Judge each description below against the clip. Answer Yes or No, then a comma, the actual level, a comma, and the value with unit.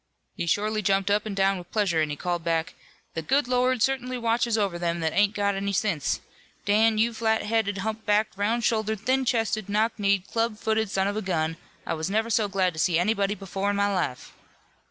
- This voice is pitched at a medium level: No, high, 205 Hz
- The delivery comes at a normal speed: No, fast, 215 wpm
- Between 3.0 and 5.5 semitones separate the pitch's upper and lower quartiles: No, narrow, 2.6 semitones